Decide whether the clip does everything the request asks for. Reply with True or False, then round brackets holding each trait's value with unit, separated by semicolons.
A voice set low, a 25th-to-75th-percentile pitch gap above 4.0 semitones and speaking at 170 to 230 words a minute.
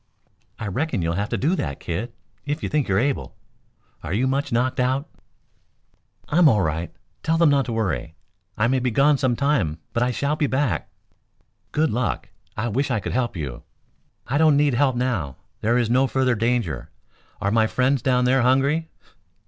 True (125 Hz; 4.6 semitones; 190 wpm)